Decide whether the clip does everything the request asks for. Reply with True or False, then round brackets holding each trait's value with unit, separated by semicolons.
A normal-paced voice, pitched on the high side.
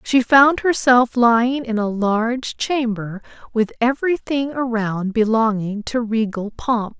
False (130 wpm; 235 Hz)